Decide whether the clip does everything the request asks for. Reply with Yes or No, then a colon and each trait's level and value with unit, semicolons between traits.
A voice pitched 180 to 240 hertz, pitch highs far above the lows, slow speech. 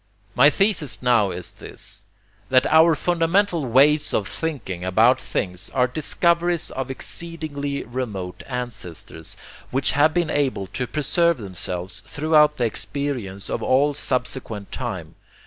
No: low, 135 Hz; wide, 6.3 semitones; slow, 130 wpm